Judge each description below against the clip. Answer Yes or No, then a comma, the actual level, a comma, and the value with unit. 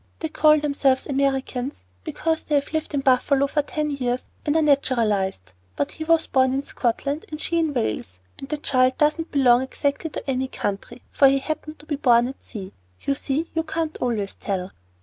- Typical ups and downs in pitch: Yes, average, 3.4 semitones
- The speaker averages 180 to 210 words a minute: Yes, average, 195 wpm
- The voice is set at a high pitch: Yes, very high, 275 Hz